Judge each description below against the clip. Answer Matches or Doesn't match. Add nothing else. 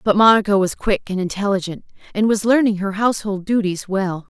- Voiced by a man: Doesn't match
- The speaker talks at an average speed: Matches